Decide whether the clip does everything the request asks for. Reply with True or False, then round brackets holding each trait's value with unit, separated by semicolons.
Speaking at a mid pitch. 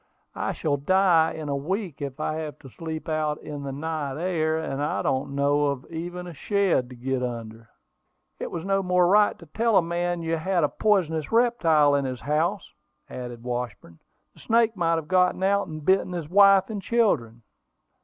True (160 Hz)